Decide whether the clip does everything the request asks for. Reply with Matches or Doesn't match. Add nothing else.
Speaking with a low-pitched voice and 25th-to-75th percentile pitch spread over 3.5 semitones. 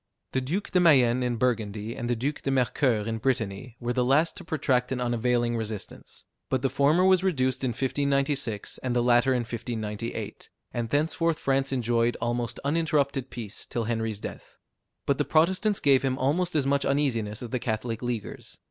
Doesn't match